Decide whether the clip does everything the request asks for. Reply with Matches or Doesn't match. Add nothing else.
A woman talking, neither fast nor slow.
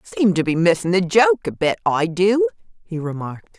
Matches